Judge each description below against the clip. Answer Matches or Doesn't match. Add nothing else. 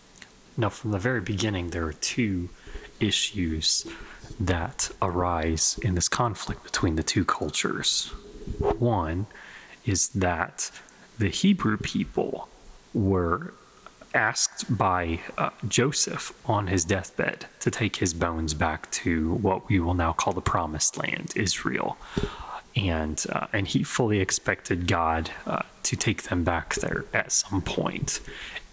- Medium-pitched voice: Doesn't match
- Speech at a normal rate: Doesn't match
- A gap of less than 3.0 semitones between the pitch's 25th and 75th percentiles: Doesn't match